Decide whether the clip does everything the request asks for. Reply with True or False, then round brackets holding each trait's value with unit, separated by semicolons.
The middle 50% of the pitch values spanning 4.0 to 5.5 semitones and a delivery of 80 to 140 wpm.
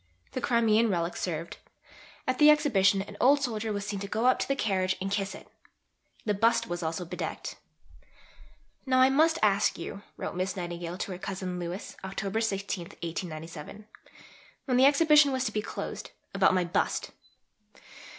False (4.4 semitones; 170 wpm)